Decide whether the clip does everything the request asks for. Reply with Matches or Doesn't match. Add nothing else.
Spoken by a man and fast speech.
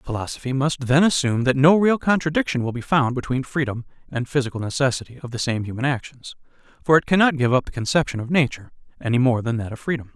Matches